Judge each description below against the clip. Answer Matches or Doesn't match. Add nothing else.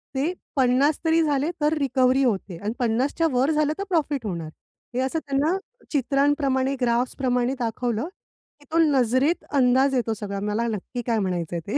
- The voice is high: Matches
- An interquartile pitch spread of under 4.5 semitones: Matches